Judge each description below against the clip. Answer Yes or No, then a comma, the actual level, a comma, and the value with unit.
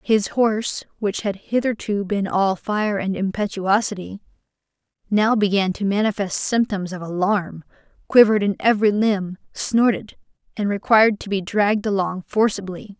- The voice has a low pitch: No, high, 200 Hz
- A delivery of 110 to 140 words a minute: Yes, slow, 135 wpm